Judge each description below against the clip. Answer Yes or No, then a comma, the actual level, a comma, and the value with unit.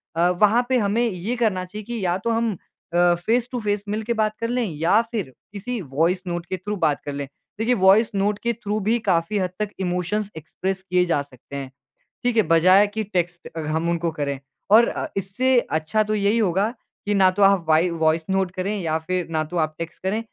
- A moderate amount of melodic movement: Yes, average, 4.0 semitones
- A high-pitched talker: Yes, high, 195 Hz